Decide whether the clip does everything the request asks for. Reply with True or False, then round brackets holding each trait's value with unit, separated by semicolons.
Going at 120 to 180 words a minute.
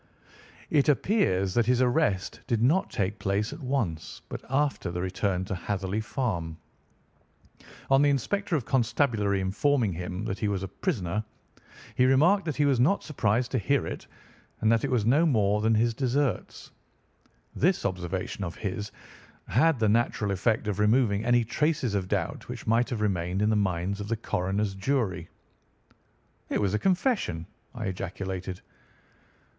True (160 wpm)